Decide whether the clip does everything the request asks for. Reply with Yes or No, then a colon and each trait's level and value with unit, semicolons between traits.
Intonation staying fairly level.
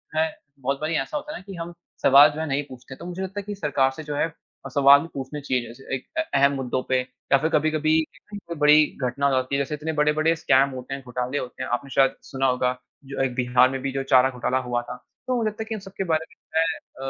No: average, 3.3 semitones